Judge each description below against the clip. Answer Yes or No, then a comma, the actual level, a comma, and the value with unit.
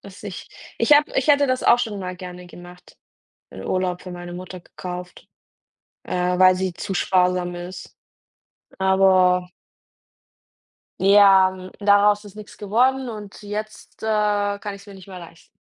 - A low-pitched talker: No, high, 190 Hz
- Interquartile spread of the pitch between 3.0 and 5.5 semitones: No, narrow, 2.4 semitones